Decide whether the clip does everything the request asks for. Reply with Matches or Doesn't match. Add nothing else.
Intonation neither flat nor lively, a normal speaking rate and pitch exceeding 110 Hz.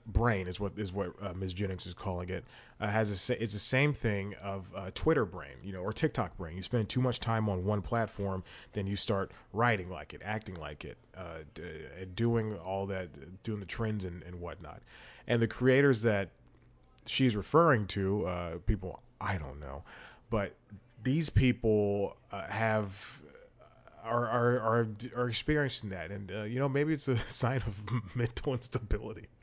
Doesn't match